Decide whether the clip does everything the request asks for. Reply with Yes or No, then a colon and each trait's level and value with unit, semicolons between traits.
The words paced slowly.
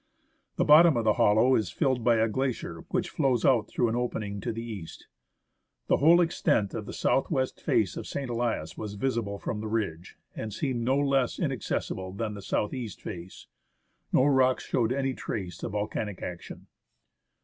No: average, 180 wpm